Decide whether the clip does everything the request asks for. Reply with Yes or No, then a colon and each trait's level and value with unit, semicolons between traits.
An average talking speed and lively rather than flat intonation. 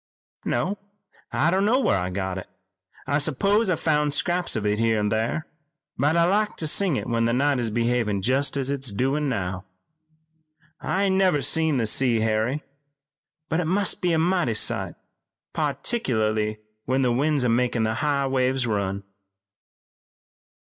Yes: average, 160 wpm; wide, 6.3 semitones